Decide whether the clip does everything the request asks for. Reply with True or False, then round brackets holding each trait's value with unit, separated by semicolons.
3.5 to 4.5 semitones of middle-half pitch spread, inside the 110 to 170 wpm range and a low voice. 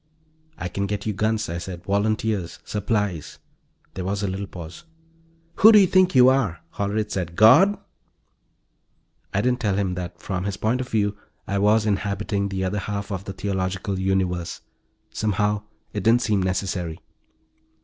False (2.4 semitones; 160 wpm; 100 Hz)